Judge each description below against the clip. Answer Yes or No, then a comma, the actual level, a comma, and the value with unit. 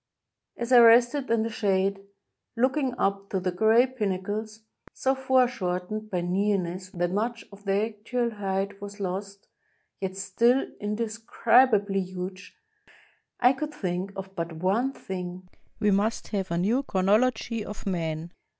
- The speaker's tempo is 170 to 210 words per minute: No, average, 140 wpm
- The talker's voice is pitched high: Yes, high, 205 Hz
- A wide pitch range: No, average, 3.6 semitones